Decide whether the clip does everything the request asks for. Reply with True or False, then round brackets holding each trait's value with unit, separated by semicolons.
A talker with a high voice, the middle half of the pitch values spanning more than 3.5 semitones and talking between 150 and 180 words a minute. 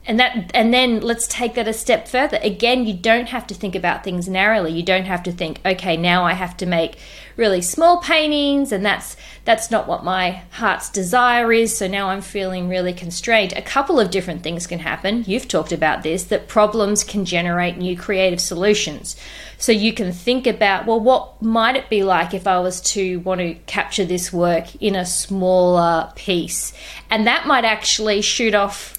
False (200 Hz; 4.0 semitones; 200 wpm)